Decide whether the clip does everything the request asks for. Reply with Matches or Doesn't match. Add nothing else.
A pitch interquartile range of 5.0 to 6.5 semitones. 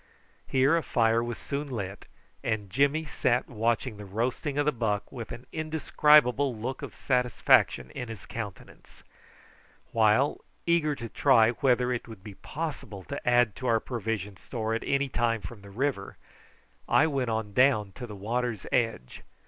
Doesn't match